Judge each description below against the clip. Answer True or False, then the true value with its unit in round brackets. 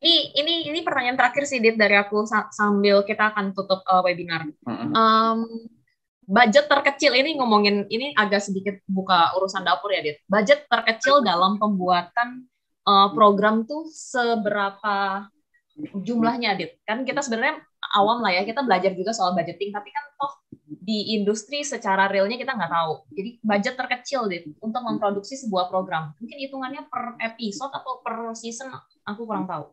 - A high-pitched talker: True (220 Hz)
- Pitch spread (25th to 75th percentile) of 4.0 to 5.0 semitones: True (4.6 semitones)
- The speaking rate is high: True (155 wpm)